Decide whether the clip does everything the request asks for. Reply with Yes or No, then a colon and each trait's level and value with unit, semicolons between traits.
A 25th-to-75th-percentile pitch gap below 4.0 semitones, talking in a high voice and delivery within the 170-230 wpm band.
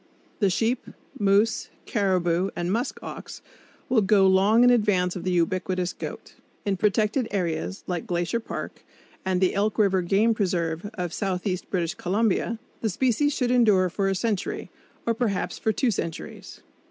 No: average, 3.5 semitones; high, 195 Hz; average, 155 wpm